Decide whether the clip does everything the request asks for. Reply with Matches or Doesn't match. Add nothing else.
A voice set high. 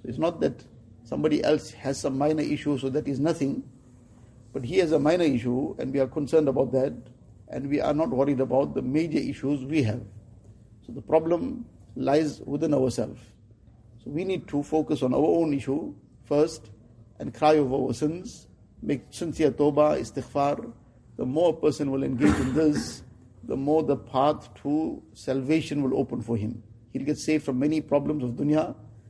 Doesn't match